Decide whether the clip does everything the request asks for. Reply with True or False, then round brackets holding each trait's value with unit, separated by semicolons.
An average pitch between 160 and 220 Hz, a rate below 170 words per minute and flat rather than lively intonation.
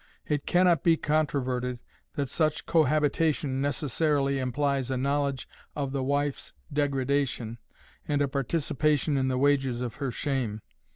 False (140 Hz; 135 wpm; 2.1 semitones)